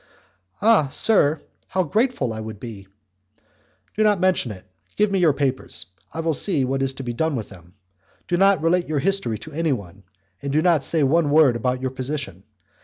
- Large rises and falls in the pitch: Yes, wide, 5.7 semitones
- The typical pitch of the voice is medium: Yes, medium, 145 Hz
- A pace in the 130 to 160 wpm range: No, average, 190 wpm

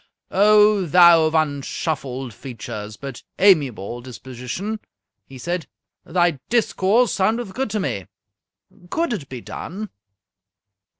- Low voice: No, medium, 165 Hz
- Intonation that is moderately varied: No, wide, 7.7 semitones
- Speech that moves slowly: Yes, slow, 110 wpm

